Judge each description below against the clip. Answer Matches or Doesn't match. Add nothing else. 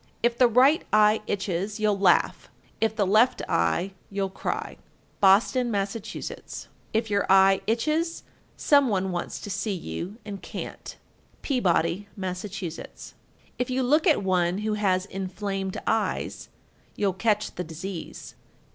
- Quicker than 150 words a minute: Doesn't match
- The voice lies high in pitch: Matches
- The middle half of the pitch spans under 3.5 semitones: Matches